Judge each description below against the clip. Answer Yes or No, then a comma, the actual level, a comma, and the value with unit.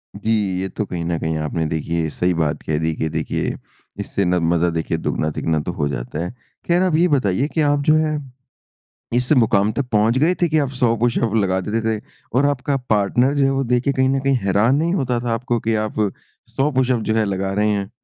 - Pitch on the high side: No, low, 110 Hz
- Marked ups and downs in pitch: Yes, wide, 6.9 semitones